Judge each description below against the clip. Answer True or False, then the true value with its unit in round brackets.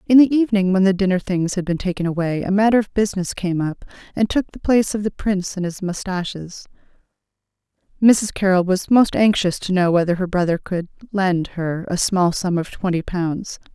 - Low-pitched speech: False (190 Hz)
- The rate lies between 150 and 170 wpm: False (200 wpm)